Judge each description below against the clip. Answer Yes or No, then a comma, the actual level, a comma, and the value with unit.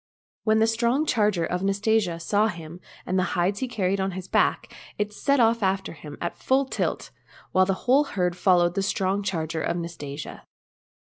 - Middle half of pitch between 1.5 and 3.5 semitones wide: No, average, 3.9 semitones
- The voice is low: No, high, 195 Hz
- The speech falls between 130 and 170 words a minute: No, average, 180 wpm